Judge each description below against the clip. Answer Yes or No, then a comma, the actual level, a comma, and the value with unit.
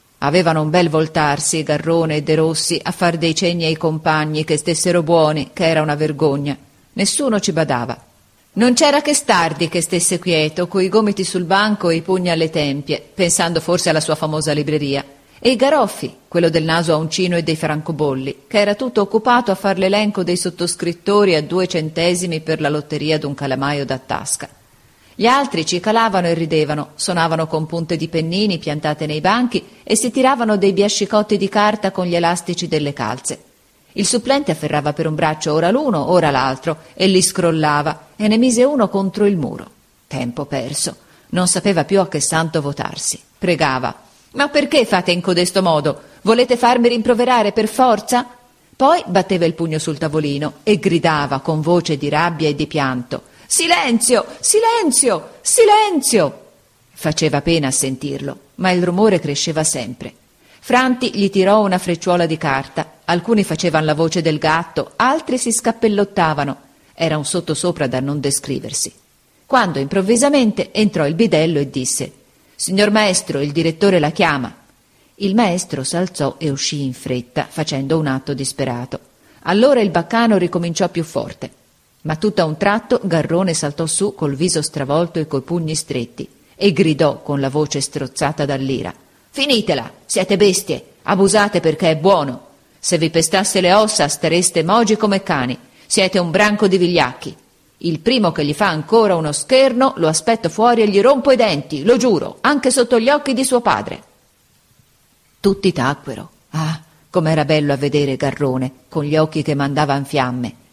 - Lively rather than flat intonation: No, average, 5.0 semitones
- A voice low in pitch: No, medium, 170 Hz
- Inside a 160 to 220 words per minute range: Yes, average, 165 wpm